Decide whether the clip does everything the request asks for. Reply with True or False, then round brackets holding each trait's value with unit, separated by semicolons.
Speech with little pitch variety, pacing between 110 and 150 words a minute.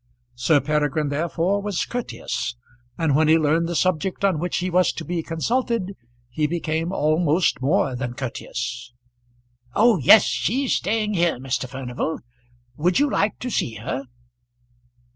False (5.6 semitones; 145 wpm)